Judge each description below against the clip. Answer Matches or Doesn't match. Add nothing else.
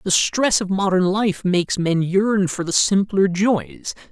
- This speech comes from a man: Matches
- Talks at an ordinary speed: Matches